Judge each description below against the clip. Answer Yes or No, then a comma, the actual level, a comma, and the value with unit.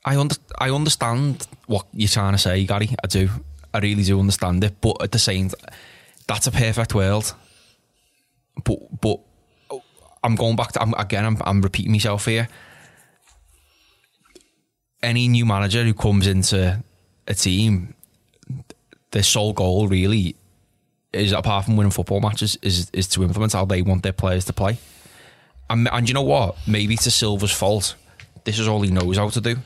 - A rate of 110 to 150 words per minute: No, average, 170 wpm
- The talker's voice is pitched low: Yes, low, 105 Hz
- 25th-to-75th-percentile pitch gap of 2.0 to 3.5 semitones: Yes, average, 3.1 semitones